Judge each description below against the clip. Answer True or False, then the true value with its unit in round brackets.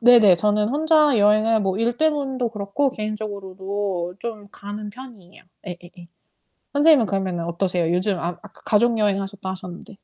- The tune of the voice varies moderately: True (3.8 semitones)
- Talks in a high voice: True (210 Hz)